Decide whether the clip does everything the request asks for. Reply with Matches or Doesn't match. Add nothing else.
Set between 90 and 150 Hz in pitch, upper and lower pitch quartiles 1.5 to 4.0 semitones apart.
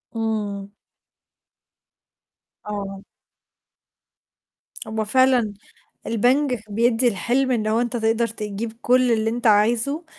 Doesn't match